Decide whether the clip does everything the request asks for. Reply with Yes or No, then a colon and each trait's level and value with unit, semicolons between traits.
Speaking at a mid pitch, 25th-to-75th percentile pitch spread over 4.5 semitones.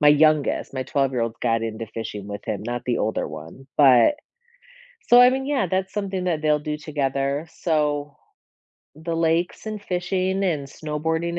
Yes: medium, 150 Hz; average, 5.2 semitones